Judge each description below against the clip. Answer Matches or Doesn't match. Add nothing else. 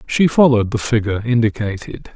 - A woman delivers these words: Doesn't match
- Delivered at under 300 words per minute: Matches